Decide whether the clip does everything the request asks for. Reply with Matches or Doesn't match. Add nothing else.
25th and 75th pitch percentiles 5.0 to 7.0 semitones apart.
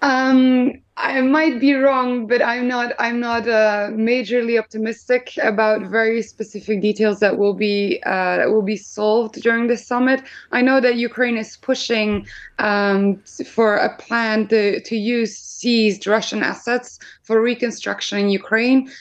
Doesn't match